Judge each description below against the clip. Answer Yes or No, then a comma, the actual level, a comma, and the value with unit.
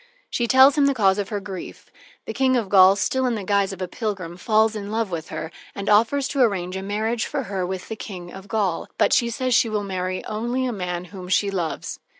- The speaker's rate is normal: No, fast, 240 wpm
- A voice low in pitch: No, high, 205 Hz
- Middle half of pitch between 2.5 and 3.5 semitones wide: No, average, 3.9 semitones